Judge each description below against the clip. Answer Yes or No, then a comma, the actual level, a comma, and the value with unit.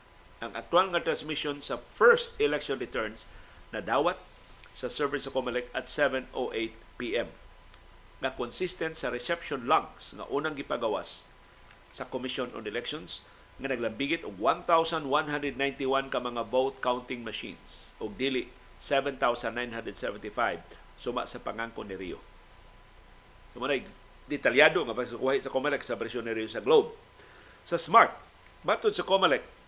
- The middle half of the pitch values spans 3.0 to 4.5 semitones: No, average, 5.1 semitones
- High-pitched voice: No, low, 135 Hz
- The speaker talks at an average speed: Yes, average, 130 wpm